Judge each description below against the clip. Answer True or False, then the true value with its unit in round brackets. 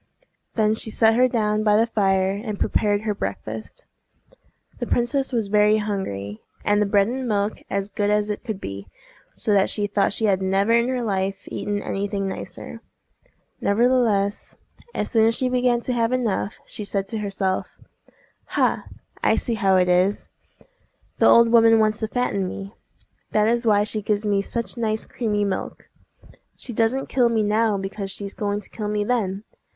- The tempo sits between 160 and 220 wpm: True (180 wpm)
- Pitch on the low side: False (210 Hz)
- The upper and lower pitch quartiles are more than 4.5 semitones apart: False (2.4 semitones)